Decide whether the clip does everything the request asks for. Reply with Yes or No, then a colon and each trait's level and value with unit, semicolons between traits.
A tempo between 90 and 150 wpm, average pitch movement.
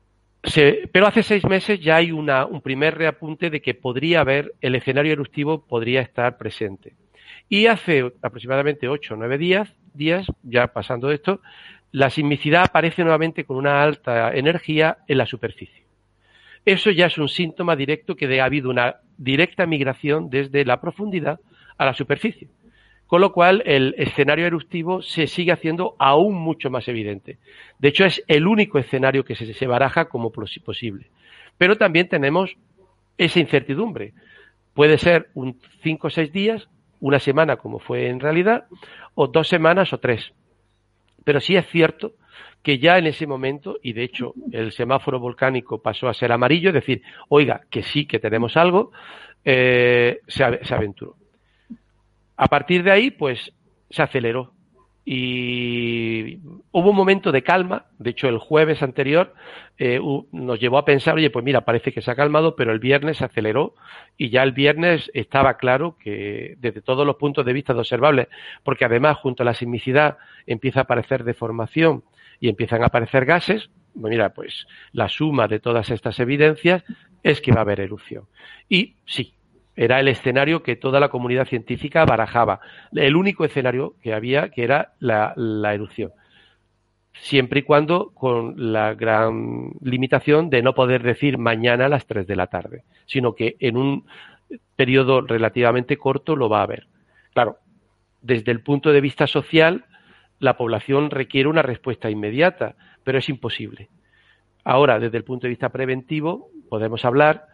No: average, 165 wpm; average, 4.8 semitones